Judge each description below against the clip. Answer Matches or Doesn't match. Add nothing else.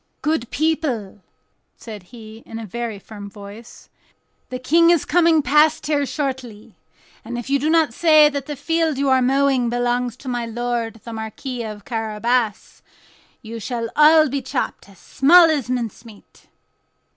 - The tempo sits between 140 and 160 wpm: Matches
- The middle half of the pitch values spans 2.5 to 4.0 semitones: Doesn't match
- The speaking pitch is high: Matches